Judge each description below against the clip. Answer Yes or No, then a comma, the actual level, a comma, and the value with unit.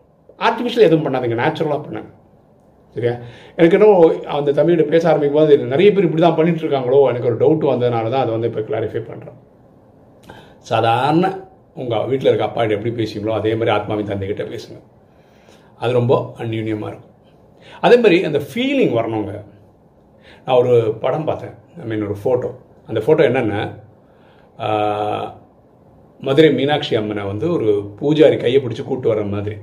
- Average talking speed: No, fast, 140 wpm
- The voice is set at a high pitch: No, low, 120 Hz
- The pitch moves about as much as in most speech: No, wide, 6.8 semitones